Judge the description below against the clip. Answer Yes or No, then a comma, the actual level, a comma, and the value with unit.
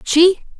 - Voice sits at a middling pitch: No, very high, 350 Hz